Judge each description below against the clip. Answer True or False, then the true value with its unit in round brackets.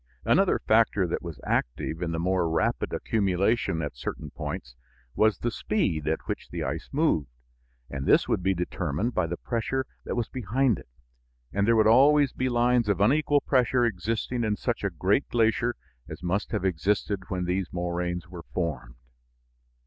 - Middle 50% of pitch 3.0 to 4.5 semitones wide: False (5.3 semitones)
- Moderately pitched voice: False (100 Hz)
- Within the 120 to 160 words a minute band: False (170 wpm)